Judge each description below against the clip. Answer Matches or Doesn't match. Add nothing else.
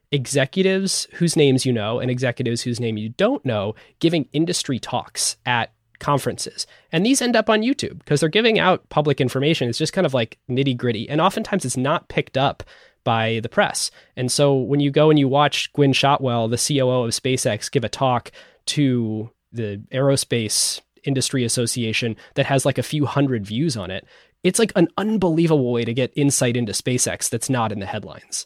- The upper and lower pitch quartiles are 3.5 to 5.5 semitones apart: Matches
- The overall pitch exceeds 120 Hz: Matches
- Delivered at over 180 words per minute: Matches